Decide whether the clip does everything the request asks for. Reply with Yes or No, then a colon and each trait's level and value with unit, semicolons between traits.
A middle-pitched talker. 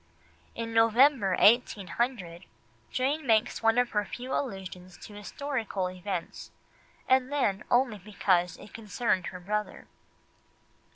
No: high, 215 Hz